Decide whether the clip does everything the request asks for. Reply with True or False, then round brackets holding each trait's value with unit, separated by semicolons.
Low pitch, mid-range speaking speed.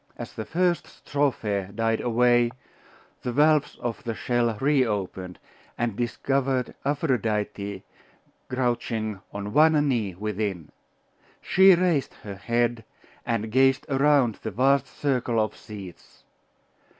False (120 Hz; 115 wpm)